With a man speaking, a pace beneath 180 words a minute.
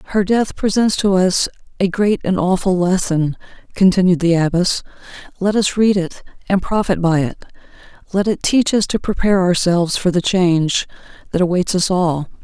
No: female; average, 170 wpm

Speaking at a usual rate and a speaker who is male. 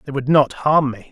No: fast, 270 wpm; male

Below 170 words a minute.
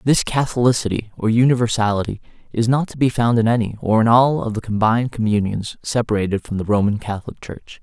No: average, 185 wpm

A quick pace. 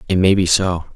Yes: fast, 255 wpm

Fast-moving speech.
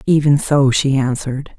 No: average, 150 wpm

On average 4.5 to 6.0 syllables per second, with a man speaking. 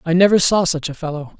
No: 6.4 syllables/s; male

